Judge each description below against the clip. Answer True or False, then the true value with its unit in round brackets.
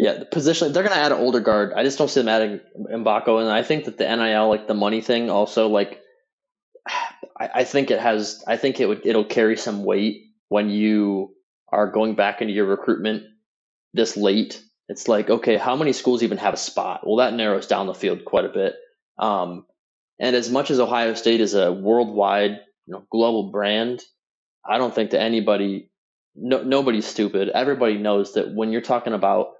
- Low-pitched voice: True (110 Hz)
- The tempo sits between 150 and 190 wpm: False (200 wpm)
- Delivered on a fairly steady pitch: False (3.3 semitones)